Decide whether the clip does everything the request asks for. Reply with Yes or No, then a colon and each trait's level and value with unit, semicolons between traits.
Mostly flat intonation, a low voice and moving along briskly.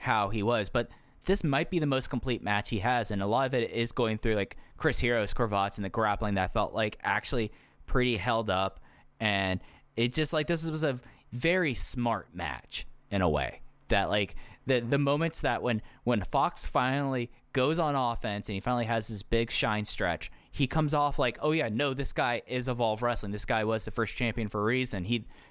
No: average, 4.0 semitones; low, 120 Hz; fast, 215 wpm